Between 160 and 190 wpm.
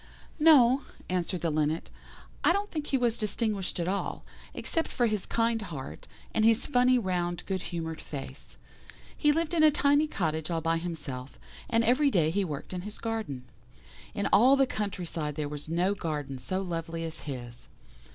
Yes: average, 180 wpm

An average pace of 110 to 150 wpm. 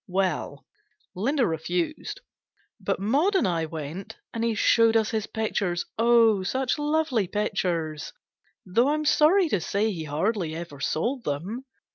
Yes: average, 145 wpm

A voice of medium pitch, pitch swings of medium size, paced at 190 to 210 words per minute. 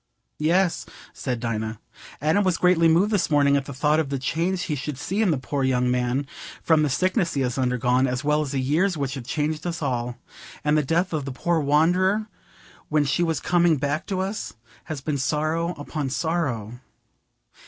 Yes: medium, 150 Hz; average, 4.3 semitones; average, 195 wpm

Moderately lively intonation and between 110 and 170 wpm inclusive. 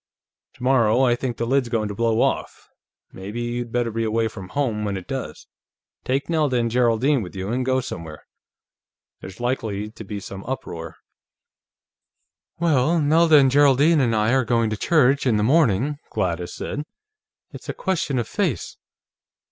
Yes: average, 4.1 semitones; average, 165 wpm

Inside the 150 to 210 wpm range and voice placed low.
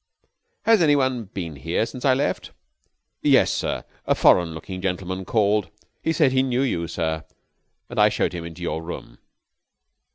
Yes: average, 165 wpm; very low, 95 Hz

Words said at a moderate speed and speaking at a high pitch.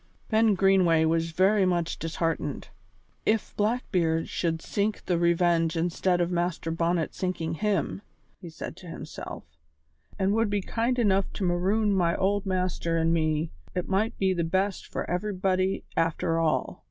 No: average, 155 wpm; medium, 180 Hz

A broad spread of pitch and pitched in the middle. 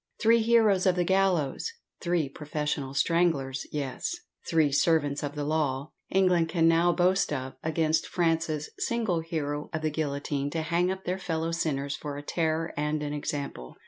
No: average, 3.2 semitones; medium, 160 Hz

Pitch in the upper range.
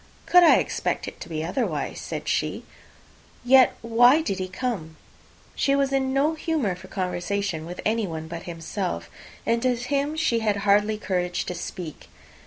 Yes: high, 210 Hz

